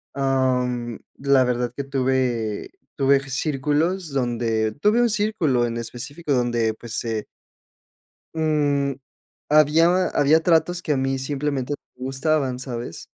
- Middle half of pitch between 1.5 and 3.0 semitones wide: No, average, 3.7 semitones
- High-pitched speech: No, low, 135 Hz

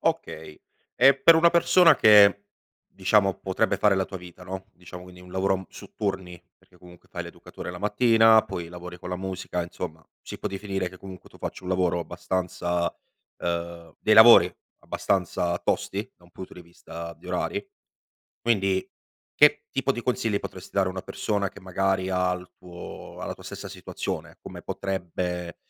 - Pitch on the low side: Yes, very low, 95 Hz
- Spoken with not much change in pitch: Yes, narrow, 2.2 semitones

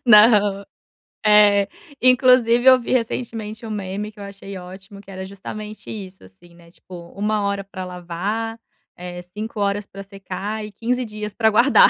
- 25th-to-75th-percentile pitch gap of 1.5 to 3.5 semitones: Yes, narrow, 2.4 semitones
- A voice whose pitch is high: Yes, high, 205 Hz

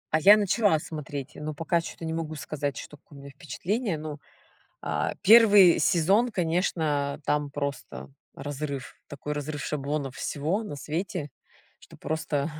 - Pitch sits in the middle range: Yes, medium, 155 Hz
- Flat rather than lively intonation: No, average, 3.3 semitones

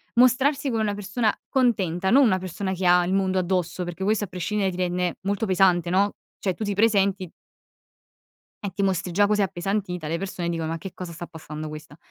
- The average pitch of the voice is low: No, high, 190 Hz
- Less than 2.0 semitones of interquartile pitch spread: No, narrow, 2.6 semitones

